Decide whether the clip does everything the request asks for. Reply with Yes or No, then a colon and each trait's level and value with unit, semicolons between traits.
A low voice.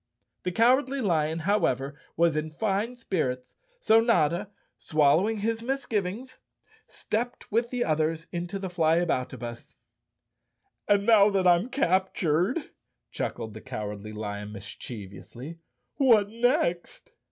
No: medium, 180 Hz